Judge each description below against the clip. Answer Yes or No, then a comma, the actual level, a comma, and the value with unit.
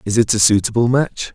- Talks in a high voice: No, low, 115 Hz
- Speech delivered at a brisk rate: Yes, fast, 225 wpm